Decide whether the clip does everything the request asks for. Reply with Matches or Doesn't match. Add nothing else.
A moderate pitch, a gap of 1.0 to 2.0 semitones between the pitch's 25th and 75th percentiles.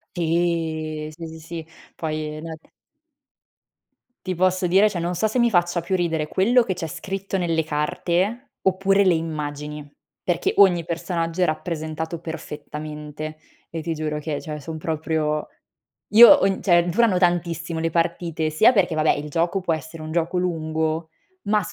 Doesn't match